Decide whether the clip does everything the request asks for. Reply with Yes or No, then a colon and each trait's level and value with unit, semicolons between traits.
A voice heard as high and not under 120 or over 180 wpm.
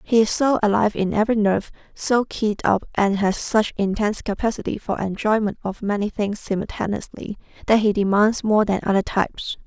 Yes: high, 210 Hz; average, 175 wpm